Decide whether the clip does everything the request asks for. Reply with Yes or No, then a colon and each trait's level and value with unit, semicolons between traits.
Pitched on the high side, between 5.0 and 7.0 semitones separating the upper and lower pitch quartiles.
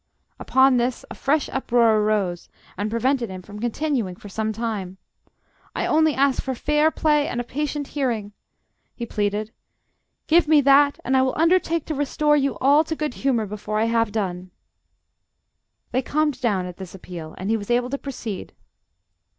Yes: high, 245 Hz; wide, 5.4 semitones